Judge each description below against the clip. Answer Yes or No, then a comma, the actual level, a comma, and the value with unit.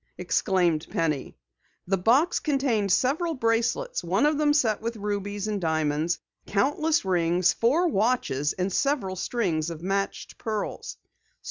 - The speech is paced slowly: Yes, slow, 130 wpm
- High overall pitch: Yes, high, 205 Hz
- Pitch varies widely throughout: Yes, wide, 7.0 semitones